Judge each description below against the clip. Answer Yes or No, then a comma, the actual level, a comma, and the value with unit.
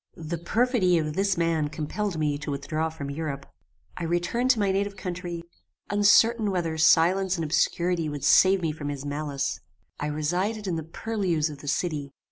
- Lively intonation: No, average, 4.1 semitones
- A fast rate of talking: No, average, 175 wpm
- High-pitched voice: No, medium, 165 Hz